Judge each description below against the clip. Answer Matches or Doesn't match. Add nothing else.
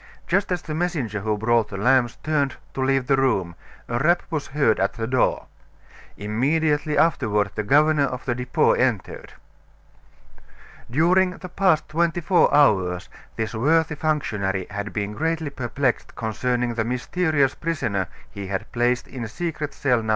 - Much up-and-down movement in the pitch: Matches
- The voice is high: Doesn't match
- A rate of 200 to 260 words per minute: Doesn't match